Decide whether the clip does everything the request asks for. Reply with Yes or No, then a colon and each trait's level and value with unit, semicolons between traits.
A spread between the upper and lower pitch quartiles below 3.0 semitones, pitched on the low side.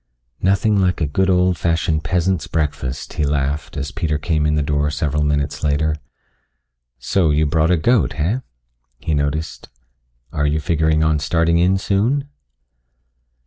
No: average, 3.4 semitones; very low, 80 Hz